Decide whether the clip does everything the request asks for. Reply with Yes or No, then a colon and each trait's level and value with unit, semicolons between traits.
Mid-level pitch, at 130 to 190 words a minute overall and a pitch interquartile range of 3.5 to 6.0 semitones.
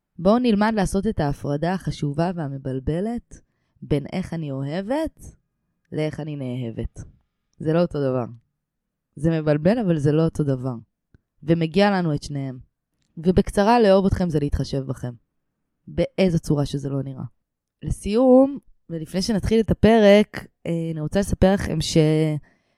Yes: medium, 160 Hz; average, 135 wpm; average, 4.9 semitones